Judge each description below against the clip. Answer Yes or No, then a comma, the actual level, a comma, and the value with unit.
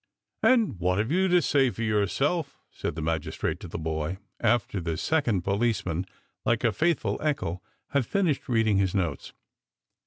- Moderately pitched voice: No, low, 110 Hz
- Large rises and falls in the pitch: Yes, wide, 7.8 semitones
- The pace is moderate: Yes, average, 175 wpm